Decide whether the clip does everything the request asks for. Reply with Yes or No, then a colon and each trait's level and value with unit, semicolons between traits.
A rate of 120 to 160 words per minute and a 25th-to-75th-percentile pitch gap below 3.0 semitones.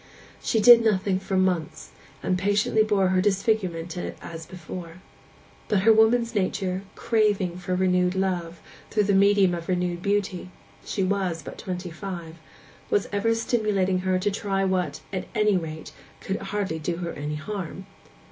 Yes: average, 155 wpm; narrow, 2.4 semitones